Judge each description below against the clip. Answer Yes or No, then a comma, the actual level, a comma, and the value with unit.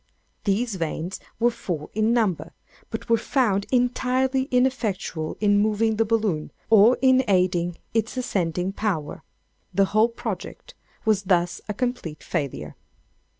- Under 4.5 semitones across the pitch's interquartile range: No, average, 4.8 semitones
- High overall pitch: Yes, high, 210 Hz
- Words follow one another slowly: Yes, slow, 130 wpm